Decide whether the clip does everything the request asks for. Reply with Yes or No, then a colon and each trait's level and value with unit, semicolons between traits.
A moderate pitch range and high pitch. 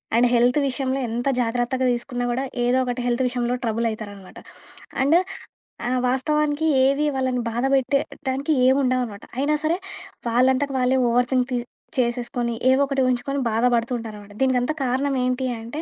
No: narrow, 2.0 semitones; very high, 250 Hz